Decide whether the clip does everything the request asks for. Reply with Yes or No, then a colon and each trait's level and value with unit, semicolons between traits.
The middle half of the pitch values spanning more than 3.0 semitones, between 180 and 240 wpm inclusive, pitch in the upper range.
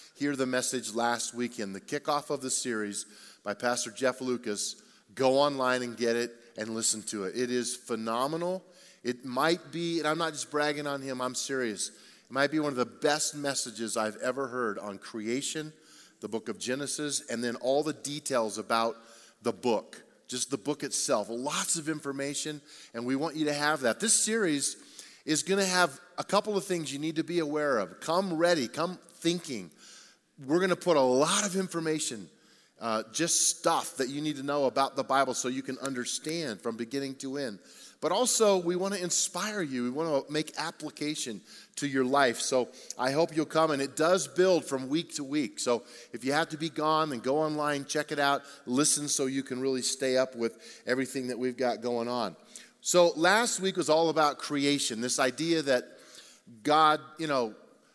No: average, 4.2 semitones; average, 200 wpm; medium, 140 Hz